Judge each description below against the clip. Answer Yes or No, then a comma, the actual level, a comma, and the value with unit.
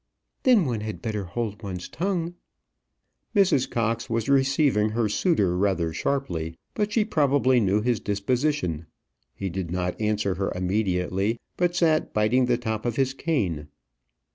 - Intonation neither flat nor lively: No, wide, 6.1 semitones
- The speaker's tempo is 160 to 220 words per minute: No, average, 145 wpm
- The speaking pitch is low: Yes, low, 110 Hz